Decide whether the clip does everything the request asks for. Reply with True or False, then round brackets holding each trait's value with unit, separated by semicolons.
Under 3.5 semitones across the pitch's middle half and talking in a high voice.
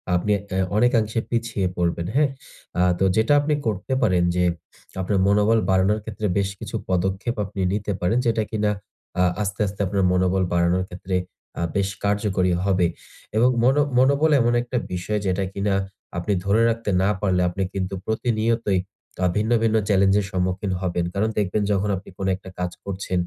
False (2.9 semitones; 100 Hz)